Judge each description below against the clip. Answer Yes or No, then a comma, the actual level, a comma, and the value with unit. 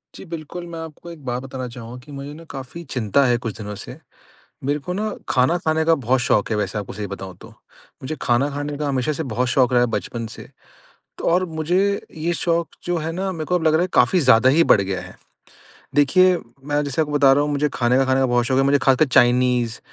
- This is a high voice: No, medium, 140 Hz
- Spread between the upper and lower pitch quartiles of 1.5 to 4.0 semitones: No, average, 4.4 semitones